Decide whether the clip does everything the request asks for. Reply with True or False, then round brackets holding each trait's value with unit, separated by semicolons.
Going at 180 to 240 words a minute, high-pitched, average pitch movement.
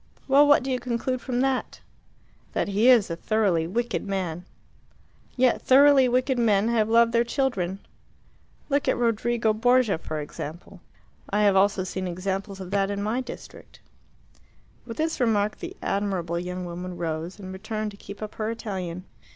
False (165 wpm; 210 Hz; 4.3 semitones)